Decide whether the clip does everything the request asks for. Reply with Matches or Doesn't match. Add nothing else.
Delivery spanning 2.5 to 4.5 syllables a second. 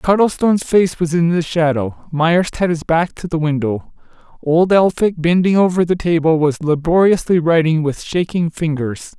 Doesn't match